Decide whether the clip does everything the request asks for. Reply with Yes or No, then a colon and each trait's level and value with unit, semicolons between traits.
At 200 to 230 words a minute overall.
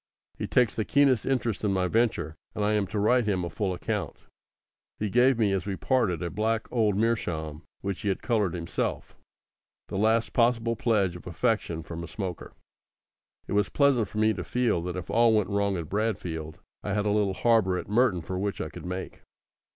Yes: fast, 205 wpm